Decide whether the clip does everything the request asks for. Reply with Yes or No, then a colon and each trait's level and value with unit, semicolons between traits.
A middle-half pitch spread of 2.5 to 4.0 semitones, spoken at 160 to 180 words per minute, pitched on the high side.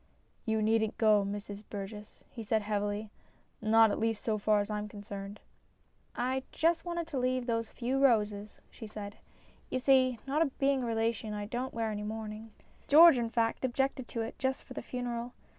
No: average, 3.4 semitones; average, 200 wpm; high, 225 Hz